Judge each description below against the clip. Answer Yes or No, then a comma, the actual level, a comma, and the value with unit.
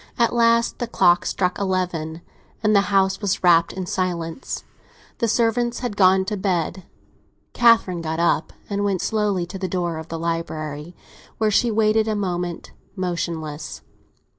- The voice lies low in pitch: No, medium, 185 Hz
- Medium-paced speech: Yes, average, 155 wpm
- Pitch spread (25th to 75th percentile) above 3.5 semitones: Yes, average, 3.9 semitones